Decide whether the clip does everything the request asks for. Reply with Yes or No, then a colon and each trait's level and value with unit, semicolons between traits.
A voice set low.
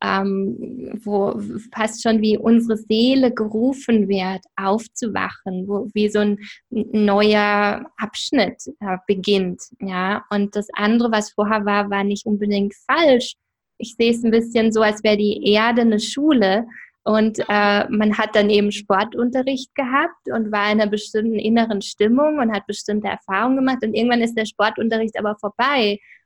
No: high, 215 Hz